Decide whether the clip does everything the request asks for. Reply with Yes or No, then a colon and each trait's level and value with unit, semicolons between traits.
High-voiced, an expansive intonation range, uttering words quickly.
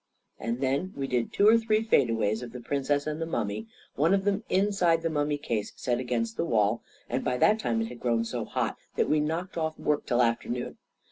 No: medium, 140 Hz; wide, 6.0 semitones; fast, 225 wpm